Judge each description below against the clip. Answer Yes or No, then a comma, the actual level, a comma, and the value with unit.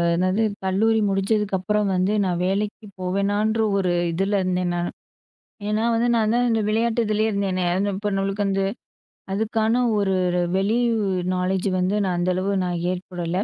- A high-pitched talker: Yes, high, 195 Hz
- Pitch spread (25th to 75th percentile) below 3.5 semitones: Yes, narrow, 2.6 semitones